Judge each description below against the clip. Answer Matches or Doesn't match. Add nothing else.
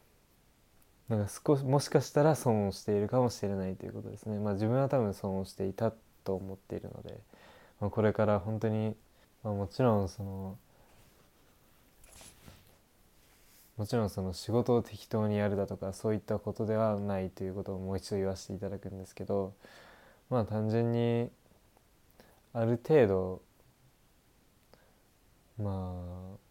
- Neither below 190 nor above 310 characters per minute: Matches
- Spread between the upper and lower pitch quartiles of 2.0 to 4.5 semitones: Matches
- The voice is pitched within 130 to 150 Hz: Doesn't match